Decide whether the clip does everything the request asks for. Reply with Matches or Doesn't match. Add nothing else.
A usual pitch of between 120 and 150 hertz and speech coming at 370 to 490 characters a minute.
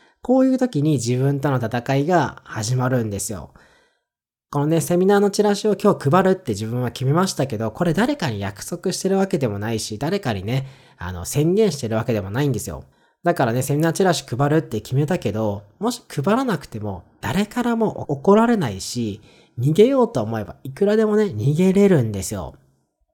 Matches